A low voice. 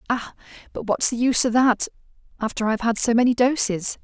No: high, 235 Hz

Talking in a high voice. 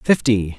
No: low, 115 Hz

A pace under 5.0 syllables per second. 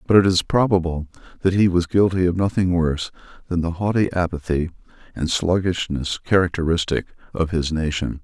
No: 5.5 syllables/s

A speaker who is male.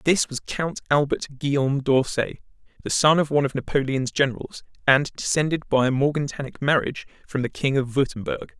Yes: male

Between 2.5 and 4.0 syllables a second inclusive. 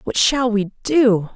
Yes: 3.3 syllables/s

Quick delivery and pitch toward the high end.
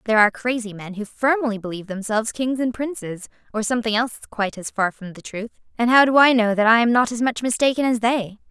Yes: fast, 240 wpm; high, 230 Hz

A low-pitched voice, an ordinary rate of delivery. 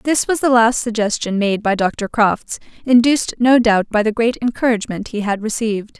No: high, 225 Hz; average, 190 wpm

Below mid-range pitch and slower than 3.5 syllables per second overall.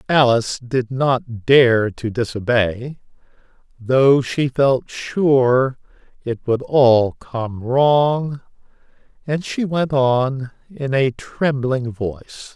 Yes: low, 130 Hz; 2.9 syllables/s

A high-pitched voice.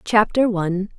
Yes: high, 205 Hz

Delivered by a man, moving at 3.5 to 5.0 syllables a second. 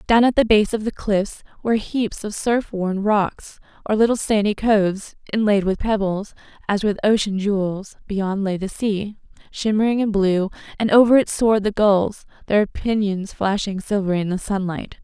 No: female; 4.7 syllables/s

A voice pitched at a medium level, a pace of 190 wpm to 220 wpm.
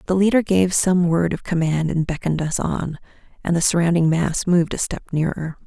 Yes: medium, 170 Hz; average, 200 wpm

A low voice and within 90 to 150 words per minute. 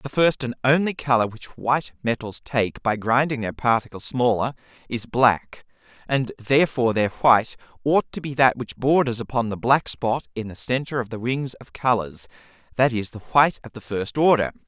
No: low, 120 Hz; average, 190 wpm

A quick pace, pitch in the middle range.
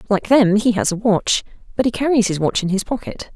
No: fast, 250 wpm; high, 205 Hz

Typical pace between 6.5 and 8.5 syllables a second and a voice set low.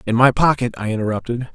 Yes: 6.6 syllables/s; low, 120 Hz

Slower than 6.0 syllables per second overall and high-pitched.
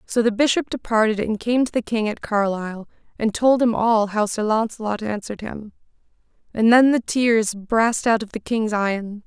Yes: 4.9 syllables/s; high, 220 Hz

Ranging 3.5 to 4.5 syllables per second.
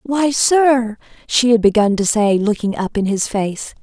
Yes: 4.1 syllables/s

